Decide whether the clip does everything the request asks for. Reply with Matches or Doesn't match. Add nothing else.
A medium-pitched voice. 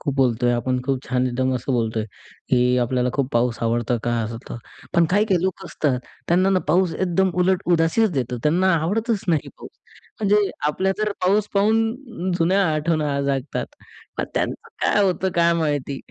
Matches